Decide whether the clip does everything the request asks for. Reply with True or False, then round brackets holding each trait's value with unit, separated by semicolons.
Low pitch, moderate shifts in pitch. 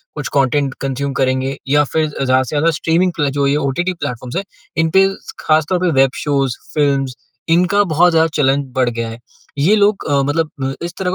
False (145 Hz; 3.7 semitones)